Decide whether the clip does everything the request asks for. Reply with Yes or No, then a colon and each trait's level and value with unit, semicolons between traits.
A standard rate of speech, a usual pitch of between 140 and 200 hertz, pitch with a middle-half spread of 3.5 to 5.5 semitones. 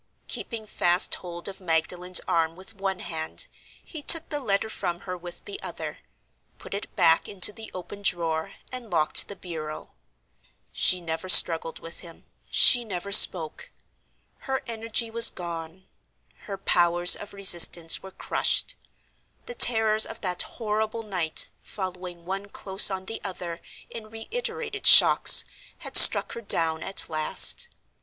Yes: average, 145 wpm; high, 190 Hz; average, 4.2 semitones